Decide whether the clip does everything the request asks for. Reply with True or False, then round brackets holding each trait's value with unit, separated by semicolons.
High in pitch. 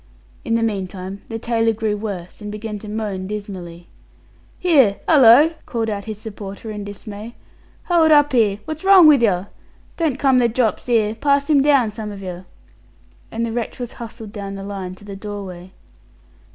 True (215 Hz)